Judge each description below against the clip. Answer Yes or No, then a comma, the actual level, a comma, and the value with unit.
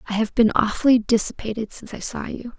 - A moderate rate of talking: No, fast, 210 wpm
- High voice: Yes, high, 225 Hz